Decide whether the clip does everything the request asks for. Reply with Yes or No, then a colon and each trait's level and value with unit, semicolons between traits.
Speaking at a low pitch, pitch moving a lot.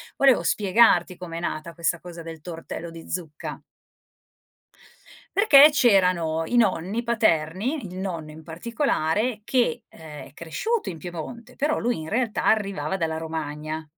No: medium, 180 Hz; wide, 6.2 semitones